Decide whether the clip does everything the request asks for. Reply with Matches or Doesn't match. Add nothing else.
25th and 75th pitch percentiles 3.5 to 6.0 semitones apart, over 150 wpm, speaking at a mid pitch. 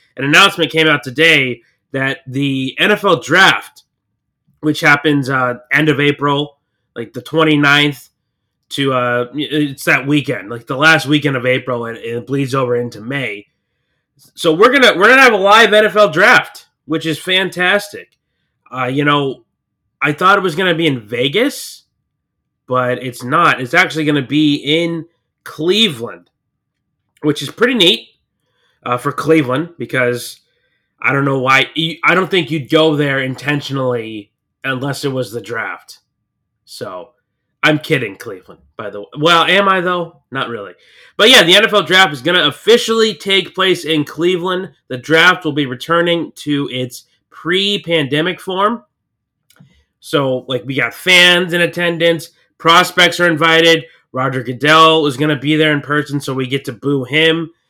Matches